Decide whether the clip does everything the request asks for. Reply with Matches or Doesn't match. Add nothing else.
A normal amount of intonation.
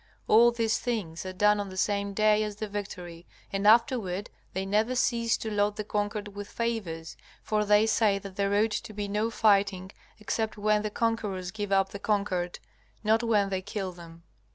Doesn't match